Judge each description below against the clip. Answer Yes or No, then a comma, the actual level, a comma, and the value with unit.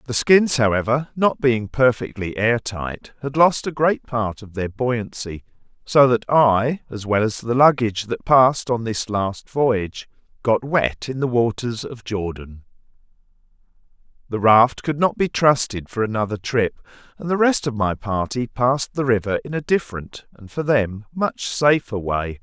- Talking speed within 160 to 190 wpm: Yes, average, 170 wpm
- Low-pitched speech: Yes, low, 120 Hz